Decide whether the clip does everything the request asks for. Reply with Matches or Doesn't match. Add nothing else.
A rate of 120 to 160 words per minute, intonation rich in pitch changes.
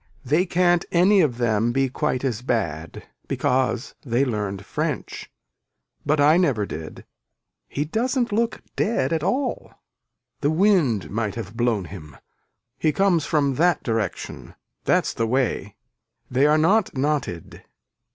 Matches